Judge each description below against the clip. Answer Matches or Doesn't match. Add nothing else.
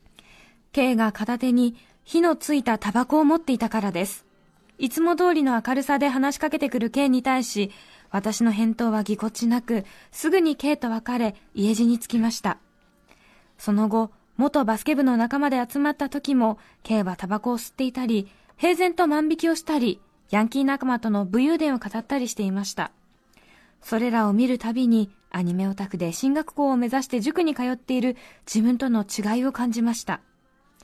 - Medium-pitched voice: Doesn't match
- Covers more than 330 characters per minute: Matches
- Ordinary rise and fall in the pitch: Matches